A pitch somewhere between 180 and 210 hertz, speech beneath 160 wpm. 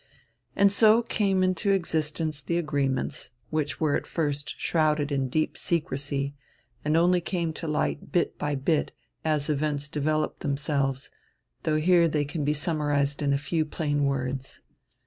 No: medium, 150 Hz; average, 150 wpm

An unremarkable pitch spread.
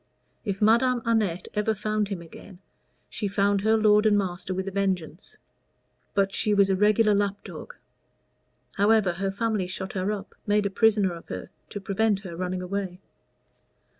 No: narrow, 2.0 semitones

